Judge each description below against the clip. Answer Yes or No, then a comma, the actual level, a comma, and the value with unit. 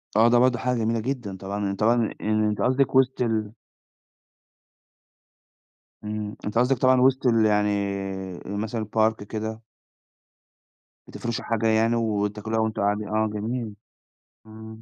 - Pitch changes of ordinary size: No, narrow, 2.0 semitones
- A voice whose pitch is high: No, low, 110 Hz